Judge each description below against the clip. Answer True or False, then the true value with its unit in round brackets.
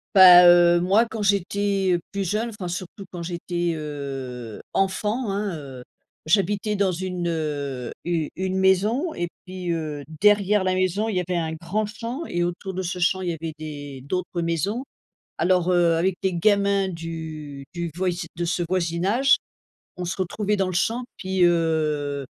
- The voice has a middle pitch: True (180 Hz)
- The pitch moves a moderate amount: True (3.0 semitones)